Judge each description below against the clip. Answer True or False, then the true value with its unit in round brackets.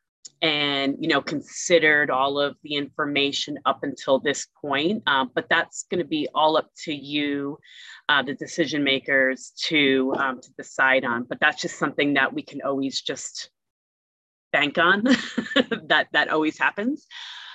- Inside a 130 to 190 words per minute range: True (155 wpm)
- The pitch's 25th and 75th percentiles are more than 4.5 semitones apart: False (2.7 semitones)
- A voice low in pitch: False (145 Hz)